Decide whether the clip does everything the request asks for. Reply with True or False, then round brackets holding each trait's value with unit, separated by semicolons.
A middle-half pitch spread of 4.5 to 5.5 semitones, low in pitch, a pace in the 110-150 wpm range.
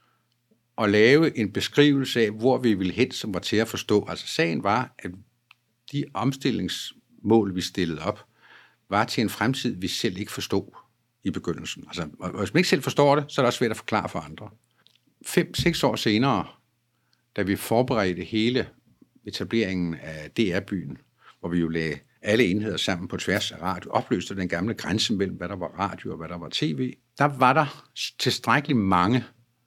False (5.1 semitones; 115 Hz; 180 wpm)